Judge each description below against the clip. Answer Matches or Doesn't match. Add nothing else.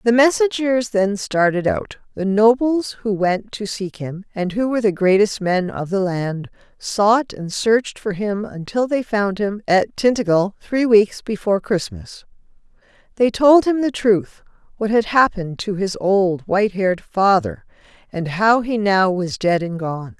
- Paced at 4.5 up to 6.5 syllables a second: Doesn't match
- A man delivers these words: Doesn't match